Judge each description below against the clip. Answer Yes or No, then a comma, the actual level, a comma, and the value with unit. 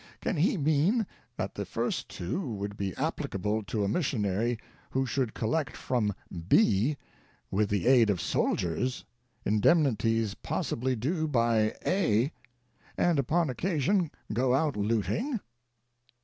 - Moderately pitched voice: No, low, 120 Hz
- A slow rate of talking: Yes, slow, 130 wpm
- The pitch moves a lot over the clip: Yes, wide, 6.5 semitones